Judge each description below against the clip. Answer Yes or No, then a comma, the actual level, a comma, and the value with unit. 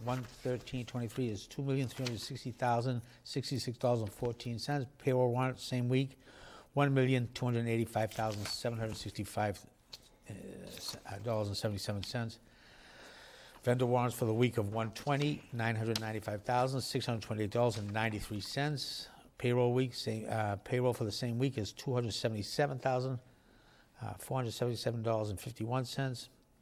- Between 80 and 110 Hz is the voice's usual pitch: No, low, 120 Hz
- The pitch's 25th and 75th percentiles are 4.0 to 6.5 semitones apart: No, narrow, 2.6 semitones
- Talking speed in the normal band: Yes, average, 160 wpm